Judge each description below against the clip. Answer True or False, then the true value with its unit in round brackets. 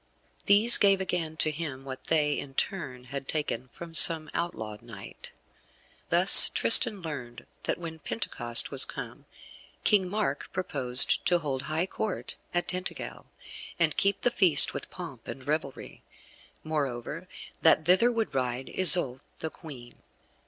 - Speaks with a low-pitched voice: False (155 Hz)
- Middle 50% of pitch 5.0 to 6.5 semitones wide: True (5.3 semitones)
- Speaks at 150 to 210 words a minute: False (140 wpm)